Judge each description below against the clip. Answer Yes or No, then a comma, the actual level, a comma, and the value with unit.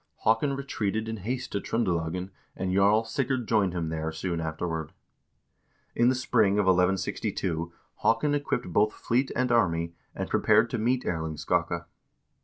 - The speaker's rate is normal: Yes, average, 155 wpm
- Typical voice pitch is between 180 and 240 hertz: No, low, 100 Hz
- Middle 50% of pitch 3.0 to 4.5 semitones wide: No, wide, 5.6 semitones